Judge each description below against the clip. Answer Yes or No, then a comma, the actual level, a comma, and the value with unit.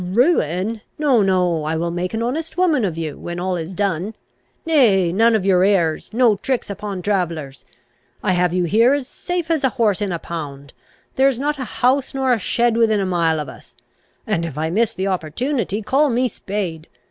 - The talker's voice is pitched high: Yes, high, 200 Hz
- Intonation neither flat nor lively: No, wide, 6.1 semitones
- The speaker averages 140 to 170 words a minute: No, fast, 205 wpm